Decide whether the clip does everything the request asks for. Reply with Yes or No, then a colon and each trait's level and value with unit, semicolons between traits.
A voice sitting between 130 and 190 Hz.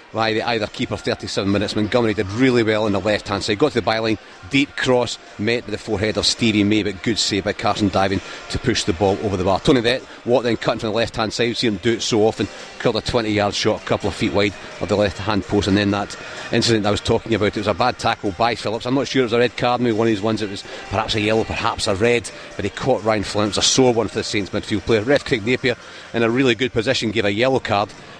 No: low, 110 Hz